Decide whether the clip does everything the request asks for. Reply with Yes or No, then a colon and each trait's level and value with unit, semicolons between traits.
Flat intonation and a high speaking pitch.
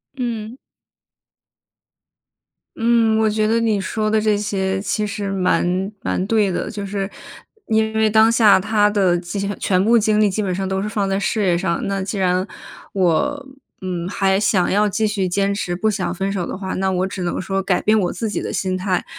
Yes: narrow, 2.3 semitones; high, 200 Hz